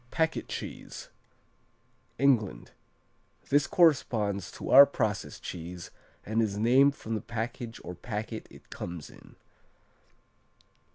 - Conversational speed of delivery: No, slow, 110 wpm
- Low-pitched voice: Yes, low, 115 Hz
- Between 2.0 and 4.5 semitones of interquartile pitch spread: No, average, 5.0 semitones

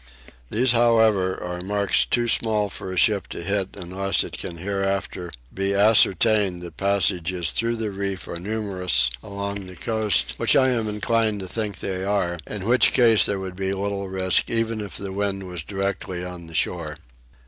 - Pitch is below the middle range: Yes, low, 100 Hz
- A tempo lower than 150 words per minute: No, average, 180 wpm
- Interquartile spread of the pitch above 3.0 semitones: No, narrow, 2.6 semitones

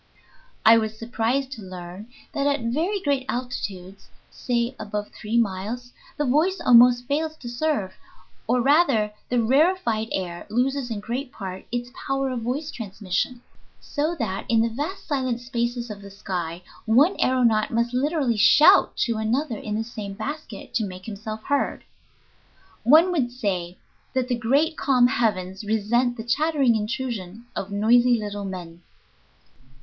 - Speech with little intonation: No, average, 4.1 semitones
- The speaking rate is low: No, average, 150 wpm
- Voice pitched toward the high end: Yes, high, 235 Hz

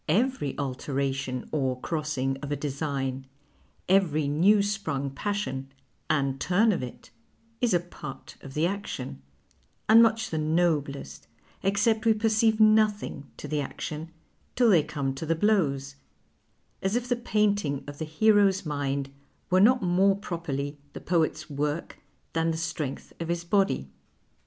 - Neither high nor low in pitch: Yes, medium, 160 Hz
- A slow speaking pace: No, average, 145 wpm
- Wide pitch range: Yes, wide, 6.5 semitones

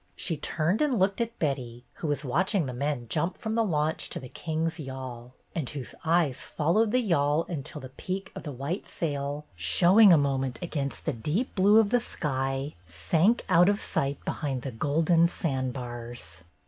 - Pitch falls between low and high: Yes, medium, 150 Hz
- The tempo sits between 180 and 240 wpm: Yes, average, 185 wpm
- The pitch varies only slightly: No, average, 5.1 semitones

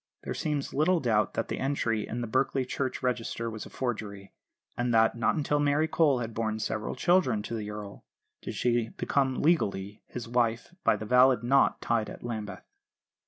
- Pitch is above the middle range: No, low, 120 Hz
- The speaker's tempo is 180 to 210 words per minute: Yes, average, 185 wpm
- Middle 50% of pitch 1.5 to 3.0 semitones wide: No, average, 3.6 semitones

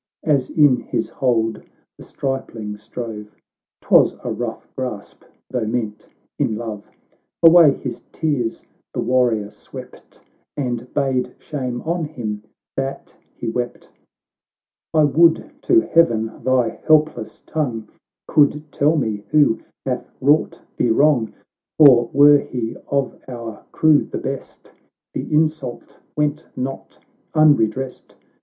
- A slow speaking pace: Yes, slow, 120 wpm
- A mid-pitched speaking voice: No, low, 130 Hz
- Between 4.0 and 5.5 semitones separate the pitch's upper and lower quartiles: Yes, average, 4.7 semitones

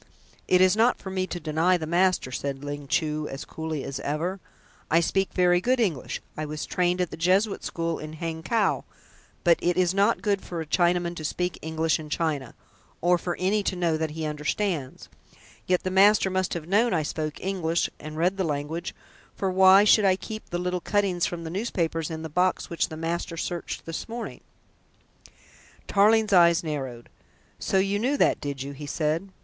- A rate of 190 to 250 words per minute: Yes, average, 195 wpm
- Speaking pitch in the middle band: Yes, medium, 175 Hz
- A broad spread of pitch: No, average, 3.2 semitones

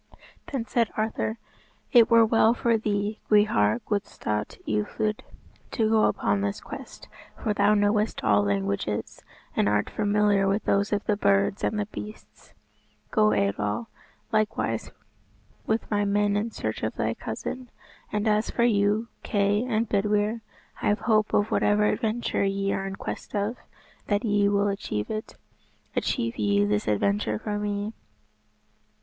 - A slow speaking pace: No, average, 150 wpm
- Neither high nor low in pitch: No, high, 205 Hz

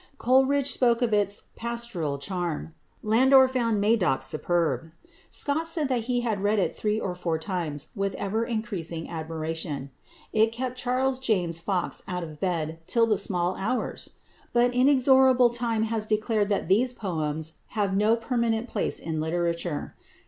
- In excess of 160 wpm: No, average, 150 wpm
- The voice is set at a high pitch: Yes, high, 210 Hz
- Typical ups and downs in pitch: No, wide, 5.9 semitones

